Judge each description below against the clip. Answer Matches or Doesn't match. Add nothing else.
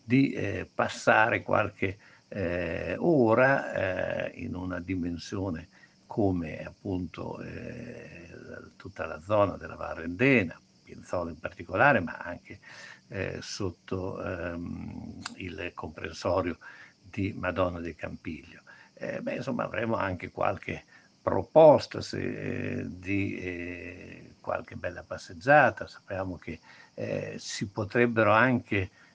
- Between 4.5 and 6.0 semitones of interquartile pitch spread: Matches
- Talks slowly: Matches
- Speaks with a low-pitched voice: Matches